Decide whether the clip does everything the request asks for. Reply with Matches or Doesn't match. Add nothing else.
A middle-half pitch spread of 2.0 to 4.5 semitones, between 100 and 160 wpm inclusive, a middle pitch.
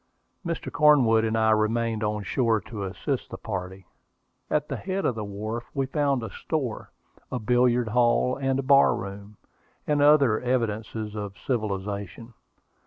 Doesn't match